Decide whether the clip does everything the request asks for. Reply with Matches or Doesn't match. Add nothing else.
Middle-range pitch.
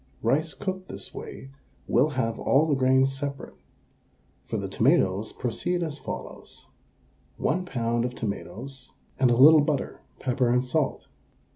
Doesn't match